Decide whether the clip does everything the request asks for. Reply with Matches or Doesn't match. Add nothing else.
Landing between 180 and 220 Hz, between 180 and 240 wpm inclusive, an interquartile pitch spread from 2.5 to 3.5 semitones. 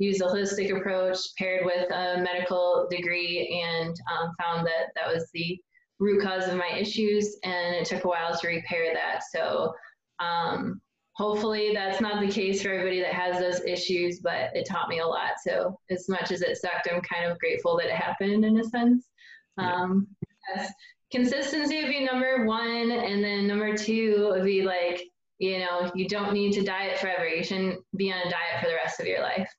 Matches